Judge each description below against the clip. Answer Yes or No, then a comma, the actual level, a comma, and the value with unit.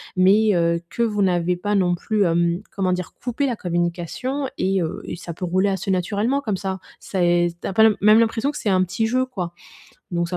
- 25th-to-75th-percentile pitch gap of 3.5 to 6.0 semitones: Yes, average, 3.9 semitones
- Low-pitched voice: No, high, 190 Hz